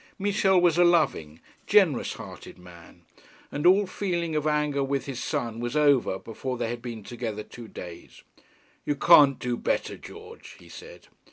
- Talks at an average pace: Yes, average, 165 wpm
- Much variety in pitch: Yes, wide, 6.5 semitones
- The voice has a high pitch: No, medium, 140 Hz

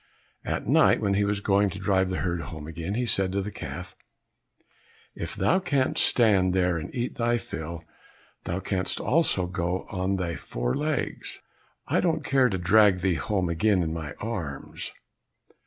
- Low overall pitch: Yes, very low, 95 Hz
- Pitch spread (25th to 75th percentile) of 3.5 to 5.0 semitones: Yes, average, 3.9 semitones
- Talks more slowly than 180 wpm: Yes, average, 170 wpm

